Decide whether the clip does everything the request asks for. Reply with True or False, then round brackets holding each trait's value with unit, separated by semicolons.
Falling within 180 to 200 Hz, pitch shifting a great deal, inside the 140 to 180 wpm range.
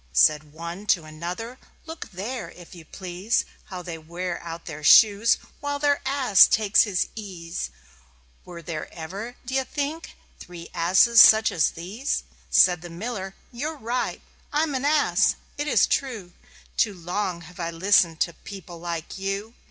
True (190 Hz; 5.8 semitones; 155 wpm)